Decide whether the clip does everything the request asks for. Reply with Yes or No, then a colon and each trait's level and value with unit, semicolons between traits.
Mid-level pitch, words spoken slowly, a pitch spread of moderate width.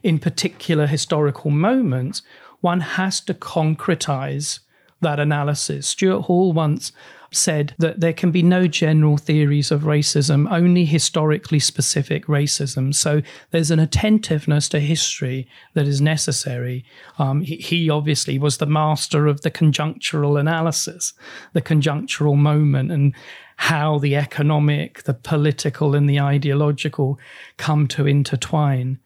No: medium, 150 Hz; slow, 130 wpm; narrow, 2.1 semitones